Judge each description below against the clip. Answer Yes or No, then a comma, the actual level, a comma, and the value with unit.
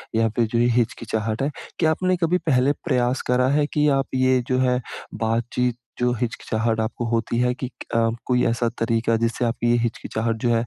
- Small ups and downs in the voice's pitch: Yes, narrow, 1.9 semitones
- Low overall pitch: Yes, low, 120 Hz